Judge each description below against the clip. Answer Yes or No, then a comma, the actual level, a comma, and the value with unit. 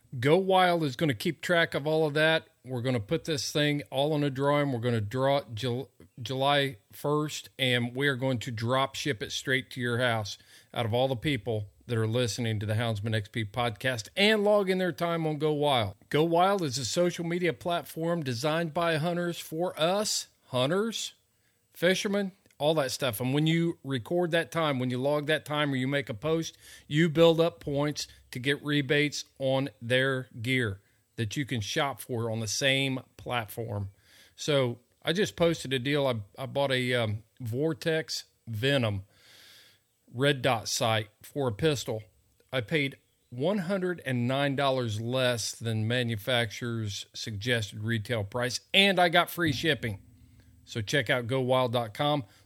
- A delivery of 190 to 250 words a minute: No, average, 170 wpm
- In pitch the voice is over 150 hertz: No, low, 135 Hz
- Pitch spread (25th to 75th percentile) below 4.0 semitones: No, average, 4.8 semitones